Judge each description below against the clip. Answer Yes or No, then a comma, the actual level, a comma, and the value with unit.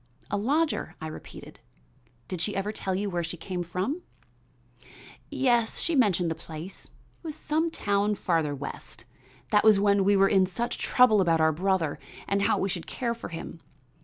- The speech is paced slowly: No, average, 180 wpm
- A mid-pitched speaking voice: No, high, 195 Hz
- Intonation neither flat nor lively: Yes, average, 4.2 semitones